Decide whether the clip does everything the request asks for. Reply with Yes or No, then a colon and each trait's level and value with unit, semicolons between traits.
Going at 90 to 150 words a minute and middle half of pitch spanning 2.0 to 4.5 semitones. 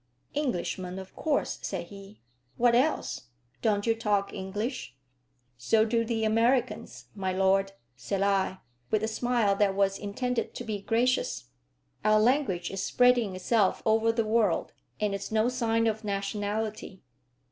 Yes: average, 145 wpm; average, 2.9 semitones